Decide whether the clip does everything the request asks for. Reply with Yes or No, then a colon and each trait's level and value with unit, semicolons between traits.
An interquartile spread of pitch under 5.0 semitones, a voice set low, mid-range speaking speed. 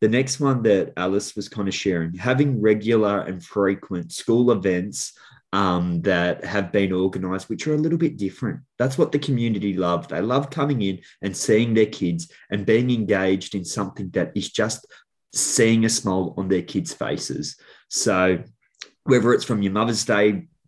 Yes: average, 3.9 semitones; low, 100 Hz; average, 175 wpm